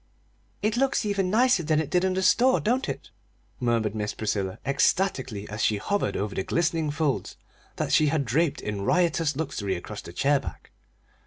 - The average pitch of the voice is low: No, medium, 150 Hz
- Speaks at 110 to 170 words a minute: No, average, 180 wpm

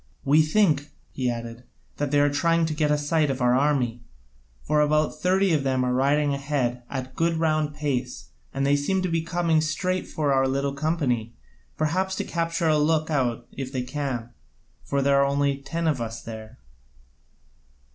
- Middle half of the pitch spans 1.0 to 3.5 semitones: Yes, average, 3.1 semitones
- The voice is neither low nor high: Yes, medium, 145 Hz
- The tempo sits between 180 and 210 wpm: Yes, average, 185 wpm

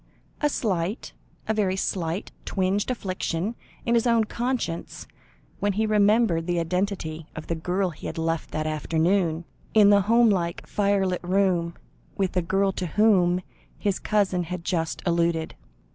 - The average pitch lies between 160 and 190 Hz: Yes, medium, 185 Hz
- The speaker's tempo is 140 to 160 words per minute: Yes, average, 145 wpm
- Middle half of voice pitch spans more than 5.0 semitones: No, average, 3.4 semitones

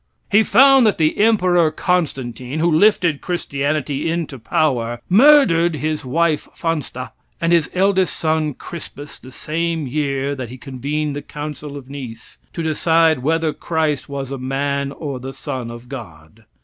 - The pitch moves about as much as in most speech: Yes, average, 3.7 semitones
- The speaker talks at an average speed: Yes, average, 150 wpm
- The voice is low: No, medium, 150 Hz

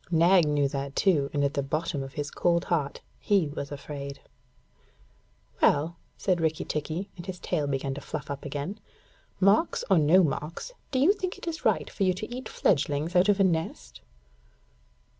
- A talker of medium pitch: Yes, medium, 160 Hz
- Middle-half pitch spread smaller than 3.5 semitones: No, average, 4.7 semitones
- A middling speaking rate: Yes, average, 180 wpm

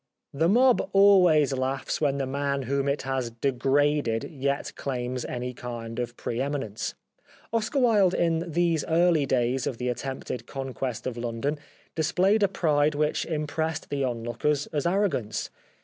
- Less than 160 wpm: Yes, average, 150 wpm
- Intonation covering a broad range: No, average, 4.4 semitones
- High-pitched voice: No, medium, 140 Hz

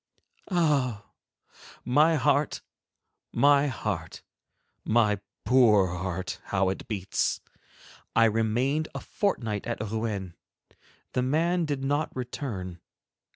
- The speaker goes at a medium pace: No, slow, 100 wpm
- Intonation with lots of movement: Yes, wide, 5.9 semitones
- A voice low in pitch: Yes, low, 120 Hz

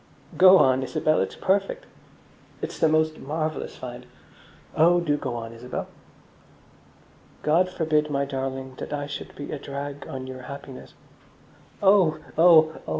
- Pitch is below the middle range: No, medium, 150 Hz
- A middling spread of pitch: Yes, average, 3.2 semitones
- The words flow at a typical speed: Yes, average, 145 wpm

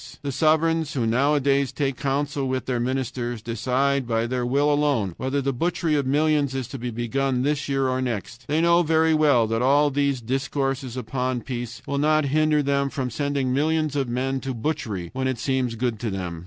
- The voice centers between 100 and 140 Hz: Yes, low, 135 Hz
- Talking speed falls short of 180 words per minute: No, average, 195 wpm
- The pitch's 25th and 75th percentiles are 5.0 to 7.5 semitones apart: No, average, 2.8 semitones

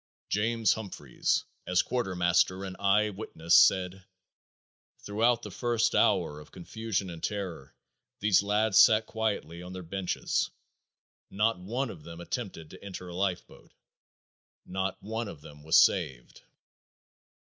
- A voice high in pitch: No, very low, 95 Hz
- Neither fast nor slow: No, slow, 130 wpm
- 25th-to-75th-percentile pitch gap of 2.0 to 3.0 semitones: No, average, 3.7 semitones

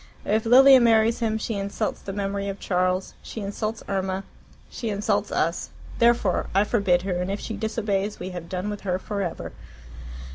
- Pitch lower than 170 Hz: No, high, 200 Hz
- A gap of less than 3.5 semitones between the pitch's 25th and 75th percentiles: Yes, narrow, 2.5 semitones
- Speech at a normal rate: Yes, average, 180 wpm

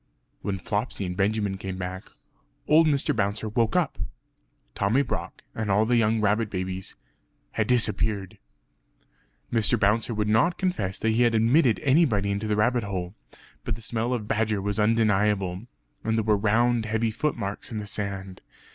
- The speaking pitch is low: Yes, low, 105 Hz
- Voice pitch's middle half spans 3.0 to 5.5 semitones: No, narrow, 2.4 semitones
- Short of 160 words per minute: No, average, 165 wpm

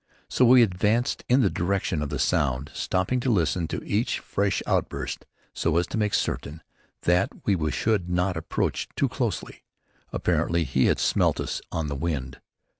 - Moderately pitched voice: No, very low, 90 Hz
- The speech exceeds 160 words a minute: Yes, average, 170 wpm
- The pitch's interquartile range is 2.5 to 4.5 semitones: No, average, 5.1 semitones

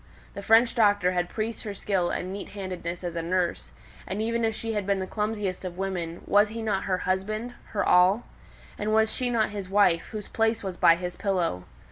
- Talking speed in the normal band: No, fast, 210 wpm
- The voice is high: Yes, high, 200 Hz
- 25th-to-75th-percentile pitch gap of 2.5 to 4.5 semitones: Yes, average, 3.0 semitones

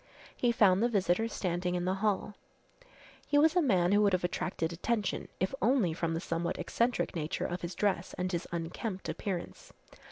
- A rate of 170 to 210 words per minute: Yes, average, 185 wpm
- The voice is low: No, medium, 185 Hz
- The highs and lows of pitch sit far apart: No, average, 3.6 semitones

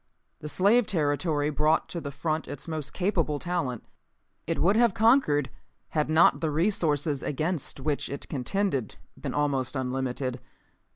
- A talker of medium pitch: Yes, medium, 150 Hz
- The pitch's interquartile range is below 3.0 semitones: No, average, 3.9 semitones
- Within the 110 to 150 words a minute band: Yes, average, 140 wpm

